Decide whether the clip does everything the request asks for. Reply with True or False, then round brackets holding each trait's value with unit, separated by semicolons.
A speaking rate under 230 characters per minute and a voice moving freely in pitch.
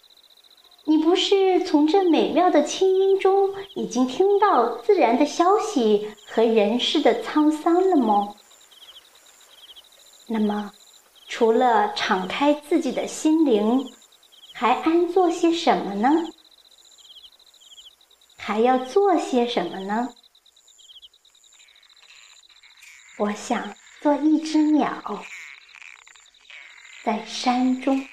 True (130 characters per minute; 7.1 semitones)